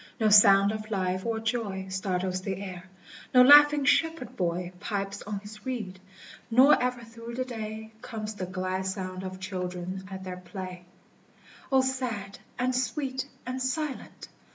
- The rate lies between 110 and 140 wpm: No, average, 155 wpm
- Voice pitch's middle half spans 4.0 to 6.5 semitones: Yes, average, 5.0 semitones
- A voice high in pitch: Yes, high, 205 Hz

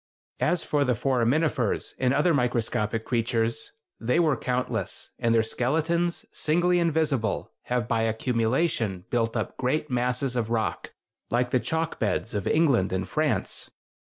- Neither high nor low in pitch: No, low, 125 Hz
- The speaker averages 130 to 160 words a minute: Yes, average, 140 wpm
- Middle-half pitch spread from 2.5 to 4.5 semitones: No, average, 5.0 semitones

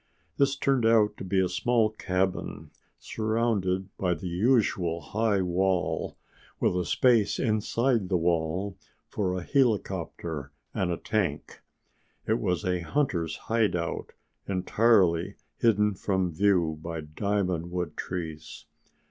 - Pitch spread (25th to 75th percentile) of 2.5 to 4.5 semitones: Yes, average, 3.8 semitones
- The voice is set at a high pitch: No, very low, 95 Hz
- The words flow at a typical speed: No, slow, 125 wpm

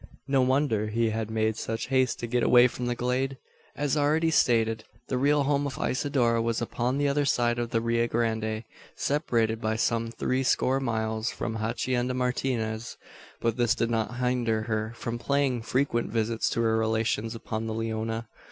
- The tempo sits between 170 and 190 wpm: Yes, average, 180 wpm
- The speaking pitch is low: Yes, low, 115 Hz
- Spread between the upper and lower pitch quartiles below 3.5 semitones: Yes, narrow, 2.4 semitones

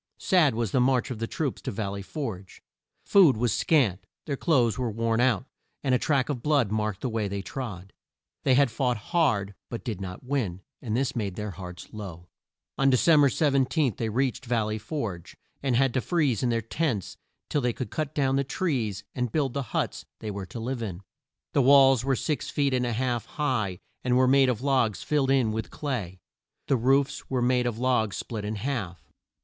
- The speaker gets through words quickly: Yes, fast, 210 wpm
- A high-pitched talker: No, low, 125 Hz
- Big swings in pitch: No, average, 4.2 semitones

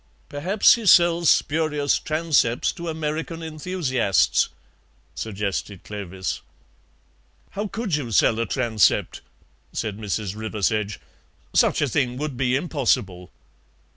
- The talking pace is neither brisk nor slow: No, slow, 105 wpm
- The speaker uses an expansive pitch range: Yes, wide, 7.0 semitones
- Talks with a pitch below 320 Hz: Yes, low, 135 Hz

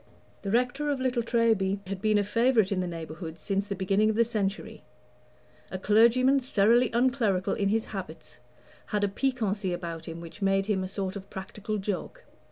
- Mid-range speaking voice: No, high, 205 Hz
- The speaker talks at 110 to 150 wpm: No, average, 180 wpm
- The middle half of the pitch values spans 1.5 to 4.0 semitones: Yes, average, 3.5 semitones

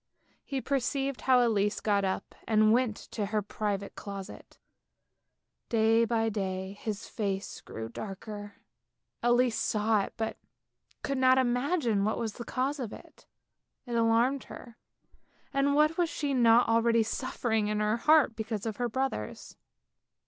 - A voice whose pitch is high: Yes, high, 225 Hz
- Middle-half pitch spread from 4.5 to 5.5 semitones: No, average, 3.4 semitones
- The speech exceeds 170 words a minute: No, average, 145 wpm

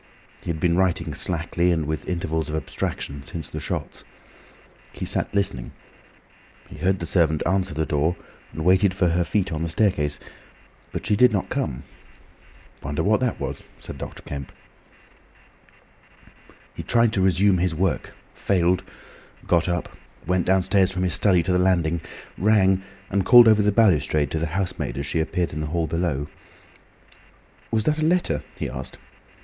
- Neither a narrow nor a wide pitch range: Yes, average, 3.4 semitones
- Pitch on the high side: No, very low, 90 Hz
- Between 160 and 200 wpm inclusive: Yes, average, 165 wpm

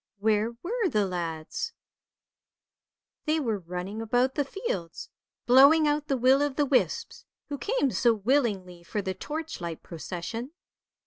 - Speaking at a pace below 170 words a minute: Yes, slow, 135 wpm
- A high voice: Yes, high, 235 Hz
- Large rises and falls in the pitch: Yes, wide, 7.5 semitones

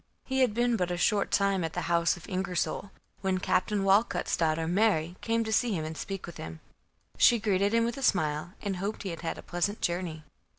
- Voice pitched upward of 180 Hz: Yes, high, 190 Hz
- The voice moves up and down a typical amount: Yes, average, 3.8 semitones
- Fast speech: Yes, fast, 220 wpm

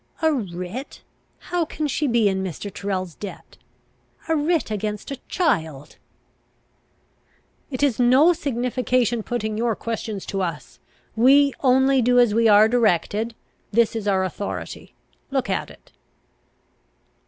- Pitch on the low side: No, high, 230 Hz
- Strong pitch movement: No, average, 4.6 semitones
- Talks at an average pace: No, slow, 130 wpm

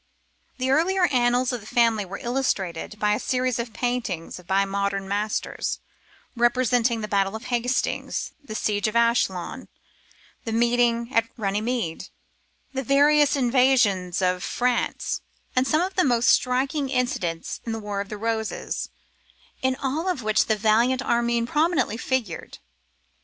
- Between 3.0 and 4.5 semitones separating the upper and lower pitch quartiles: Yes, average, 3.6 semitones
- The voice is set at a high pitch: Yes, high, 235 Hz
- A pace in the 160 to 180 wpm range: No, average, 145 wpm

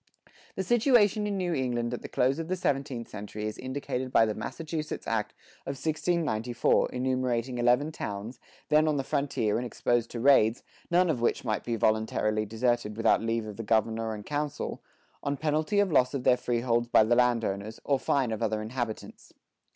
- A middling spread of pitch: Yes, average, 4.4 semitones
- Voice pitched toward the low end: Yes, low, 125 Hz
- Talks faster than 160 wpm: Yes, average, 180 wpm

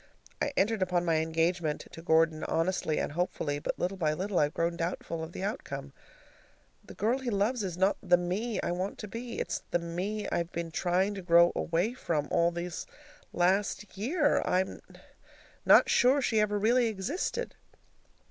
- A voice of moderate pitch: Yes, medium, 180 Hz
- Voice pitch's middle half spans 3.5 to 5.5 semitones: Yes, average, 3.8 semitones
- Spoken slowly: No, average, 175 wpm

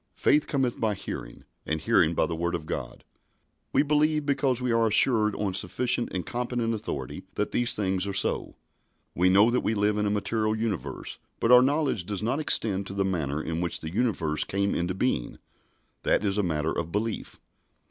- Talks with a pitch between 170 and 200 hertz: No, low, 105 Hz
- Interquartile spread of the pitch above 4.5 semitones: Yes, average, 5.3 semitones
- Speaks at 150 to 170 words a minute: No, average, 195 wpm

